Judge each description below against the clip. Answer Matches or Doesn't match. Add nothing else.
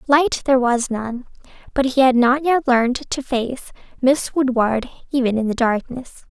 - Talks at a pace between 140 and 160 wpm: Doesn't match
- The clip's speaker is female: Matches